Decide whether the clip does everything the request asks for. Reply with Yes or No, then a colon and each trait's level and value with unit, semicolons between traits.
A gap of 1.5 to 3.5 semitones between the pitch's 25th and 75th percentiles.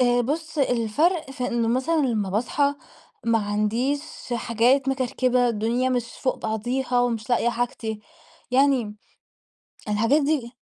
Yes: average, 2.9 semitones